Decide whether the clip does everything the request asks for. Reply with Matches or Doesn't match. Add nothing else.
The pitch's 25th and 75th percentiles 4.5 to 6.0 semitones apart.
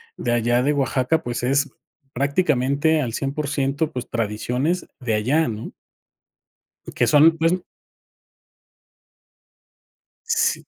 Doesn't match